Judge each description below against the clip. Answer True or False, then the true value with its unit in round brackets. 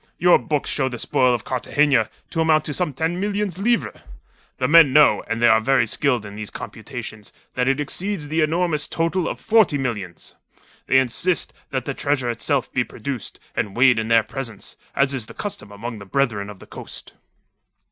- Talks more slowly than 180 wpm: False (190 wpm)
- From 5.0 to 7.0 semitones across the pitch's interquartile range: True (5.5 semitones)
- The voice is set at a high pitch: False (135 Hz)